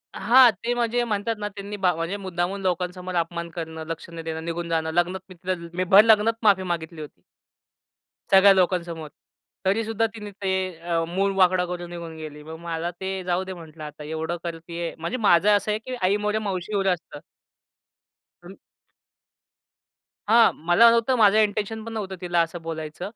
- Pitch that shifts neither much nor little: Yes, average, 3.4 semitones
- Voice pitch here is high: No, medium, 180 Hz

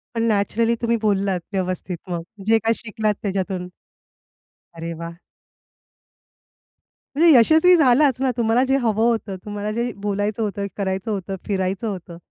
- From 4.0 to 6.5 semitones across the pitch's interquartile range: No, average, 3.3 semitones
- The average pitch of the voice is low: No, high, 210 Hz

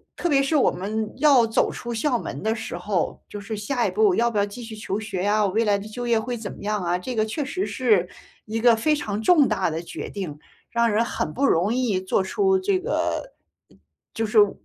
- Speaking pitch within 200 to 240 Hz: Yes, high, 220 Hz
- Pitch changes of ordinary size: Yes, average, 3.9 semitones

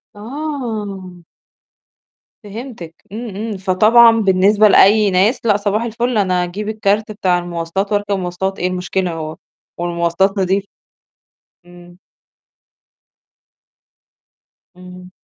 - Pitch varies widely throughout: No, average, 2.9 semitones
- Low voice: No, high, 195 Hz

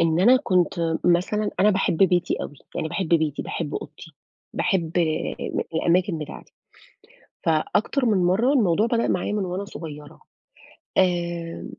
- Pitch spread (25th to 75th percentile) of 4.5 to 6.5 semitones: No, average, 3.6 semitones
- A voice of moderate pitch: Yes, medium, 175 Hz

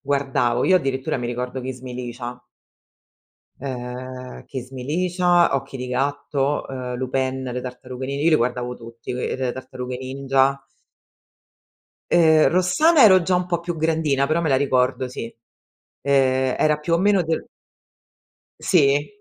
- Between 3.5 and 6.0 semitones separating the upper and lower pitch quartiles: Yes, average, 3.8 semitones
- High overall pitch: No, low, 135 Hz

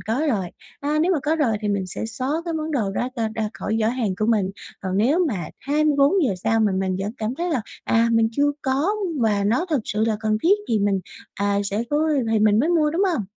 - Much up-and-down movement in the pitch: Yes, wide, 6.0 semitones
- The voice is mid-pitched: No, high, 225 Hz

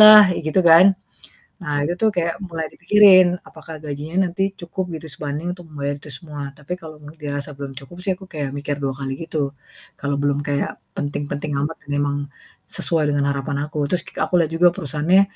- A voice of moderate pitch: Yes, medium, 155 Hz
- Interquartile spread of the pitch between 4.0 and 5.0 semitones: No, average, 3.5 semitones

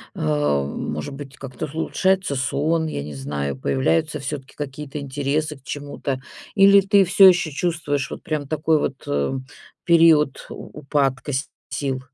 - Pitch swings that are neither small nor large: Yes, average, 3.2 semitones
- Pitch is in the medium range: Yes, medium, 145 Hz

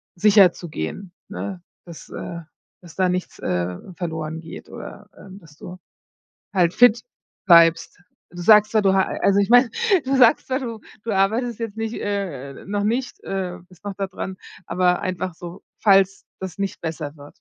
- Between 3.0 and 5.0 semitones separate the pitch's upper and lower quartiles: Yes, average, 3.4 semitones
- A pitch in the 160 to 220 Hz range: Yes, high, 190 Hz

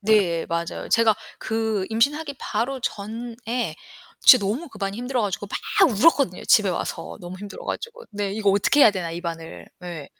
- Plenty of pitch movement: No, average, 4.3 semitones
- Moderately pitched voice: No, high, 215 Hz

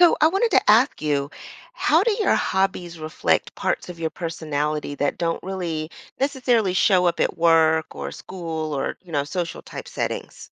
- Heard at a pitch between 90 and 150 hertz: No, medium, 170 Hz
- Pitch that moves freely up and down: No, average, 4.4 semitones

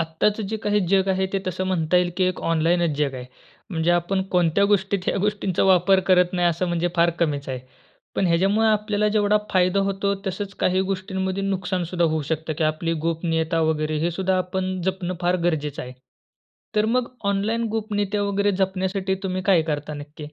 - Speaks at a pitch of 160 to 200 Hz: Yes, medium, 185 Hz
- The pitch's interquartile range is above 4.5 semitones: No, average, 2.9 semitones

